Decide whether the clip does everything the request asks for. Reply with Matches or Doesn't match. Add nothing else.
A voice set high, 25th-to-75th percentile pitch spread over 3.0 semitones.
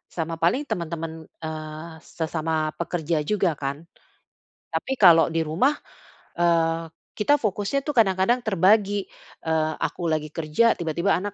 Doesn't match